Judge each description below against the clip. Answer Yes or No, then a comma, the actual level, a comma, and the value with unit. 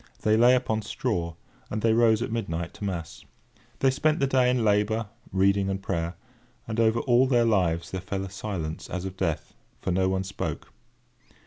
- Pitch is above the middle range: No, low, 105 Hz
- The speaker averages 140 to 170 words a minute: No, average, 190 wpm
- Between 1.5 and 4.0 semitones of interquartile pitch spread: Yes, average, 3.7 semitones